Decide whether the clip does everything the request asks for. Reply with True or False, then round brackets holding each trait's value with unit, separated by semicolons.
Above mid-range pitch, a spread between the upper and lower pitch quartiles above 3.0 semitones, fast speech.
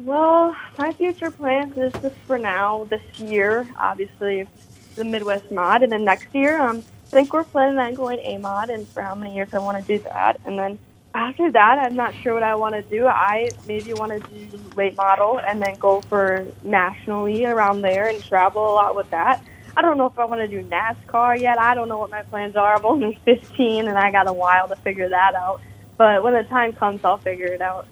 True (215 Hz; 3.6 semitones; 230 wpm)